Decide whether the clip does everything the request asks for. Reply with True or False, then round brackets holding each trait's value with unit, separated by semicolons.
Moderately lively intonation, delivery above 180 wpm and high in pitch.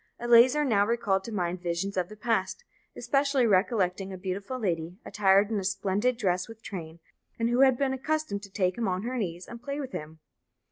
True (4.4 semitones; 200 wpm; 205 Hz)